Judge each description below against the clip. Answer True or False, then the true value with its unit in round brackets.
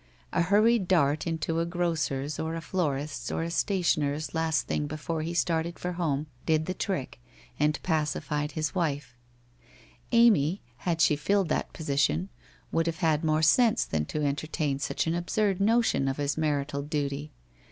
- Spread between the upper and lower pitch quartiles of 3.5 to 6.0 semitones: False (3.0 semitones)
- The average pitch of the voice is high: False (160 Hz)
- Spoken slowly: False (165 wpm)